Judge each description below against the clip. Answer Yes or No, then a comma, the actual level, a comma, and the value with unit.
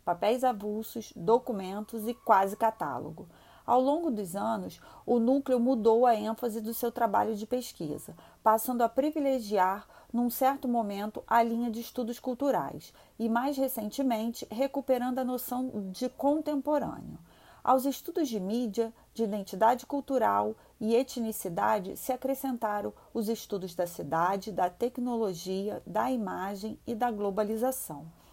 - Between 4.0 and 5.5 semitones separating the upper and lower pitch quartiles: No, average, 3.3 semitones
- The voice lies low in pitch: No, high, 230 Hz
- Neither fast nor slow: Yes, average, 130 wpm